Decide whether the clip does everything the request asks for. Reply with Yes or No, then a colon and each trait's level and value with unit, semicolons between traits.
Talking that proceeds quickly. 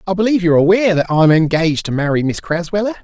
Yes: fast, 235 wpm